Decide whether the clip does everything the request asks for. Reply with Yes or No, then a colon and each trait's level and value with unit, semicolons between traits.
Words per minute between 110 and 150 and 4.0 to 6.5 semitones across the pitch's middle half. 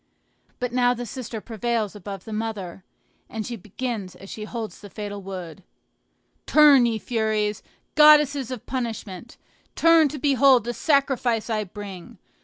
No: average, 145 wpm; average, 3.6 semitones